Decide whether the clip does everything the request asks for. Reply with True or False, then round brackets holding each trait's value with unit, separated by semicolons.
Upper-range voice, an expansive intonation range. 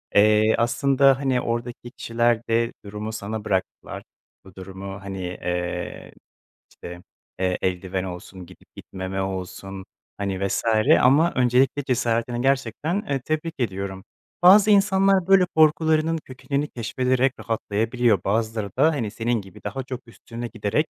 False (115 Hz; 5.7 semitones)